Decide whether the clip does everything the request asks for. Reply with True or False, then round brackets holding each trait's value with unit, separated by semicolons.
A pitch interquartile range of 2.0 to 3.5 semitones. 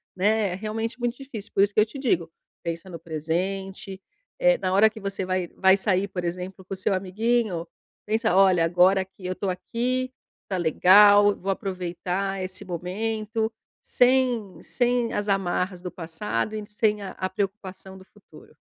True (2.9 semitones)